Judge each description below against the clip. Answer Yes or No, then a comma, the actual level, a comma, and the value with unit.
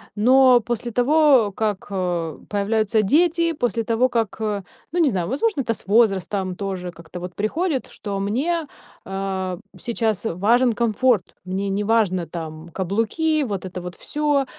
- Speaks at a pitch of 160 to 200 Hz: No, high, 215 Hz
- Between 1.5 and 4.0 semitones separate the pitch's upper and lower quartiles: No, average, 5.1 semitones